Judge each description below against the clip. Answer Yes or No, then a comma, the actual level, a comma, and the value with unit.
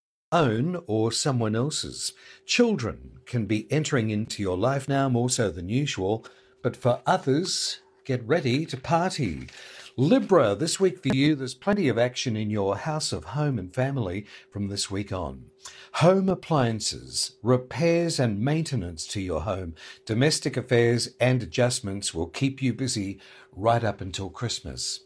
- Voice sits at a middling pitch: No, low, 125 Hz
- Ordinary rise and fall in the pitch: No, wide, 5.9 semitones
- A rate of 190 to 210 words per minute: No, average, 150 wpm